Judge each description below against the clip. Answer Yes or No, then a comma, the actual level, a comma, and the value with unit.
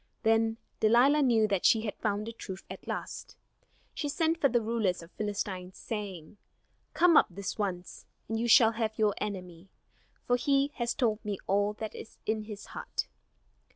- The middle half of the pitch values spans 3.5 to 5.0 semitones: No, average, 2.8 semitones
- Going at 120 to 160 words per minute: No, average, 180 wpm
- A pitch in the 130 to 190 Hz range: No, high, 215 Hz